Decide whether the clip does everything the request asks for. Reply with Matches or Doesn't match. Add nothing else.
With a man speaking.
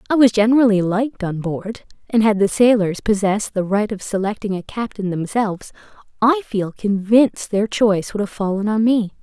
Doesn't match